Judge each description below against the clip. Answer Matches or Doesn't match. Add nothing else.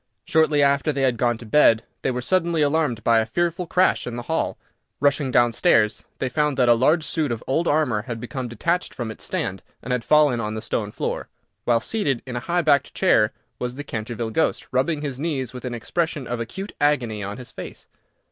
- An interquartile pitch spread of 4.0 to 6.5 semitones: Matches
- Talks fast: Matches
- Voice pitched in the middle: Doesn't match